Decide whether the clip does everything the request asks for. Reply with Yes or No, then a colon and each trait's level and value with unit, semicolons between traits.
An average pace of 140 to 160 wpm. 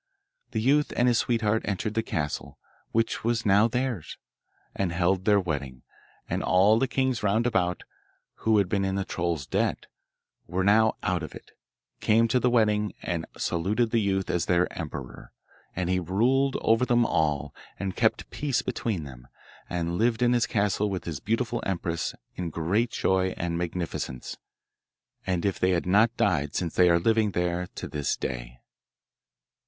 No: average, 170 wpm